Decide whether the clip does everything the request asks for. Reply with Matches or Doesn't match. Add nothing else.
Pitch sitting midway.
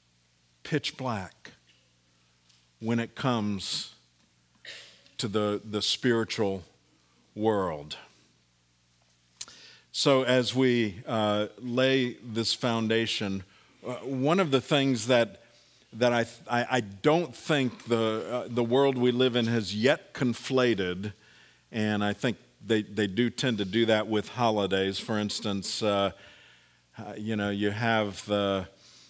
Doesn't match